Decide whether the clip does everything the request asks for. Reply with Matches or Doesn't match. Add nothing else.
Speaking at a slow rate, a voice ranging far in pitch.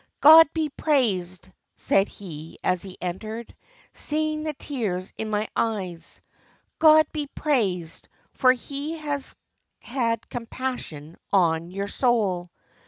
Matches